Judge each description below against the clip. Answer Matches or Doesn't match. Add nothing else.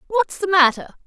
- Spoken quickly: Doesn't match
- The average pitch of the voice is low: Doesn't match